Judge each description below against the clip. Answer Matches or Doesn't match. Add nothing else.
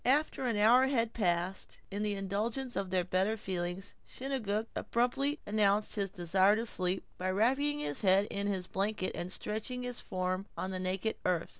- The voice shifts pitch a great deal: Doesn't match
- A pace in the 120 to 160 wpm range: Doesn't match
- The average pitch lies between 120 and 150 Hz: Doesn't match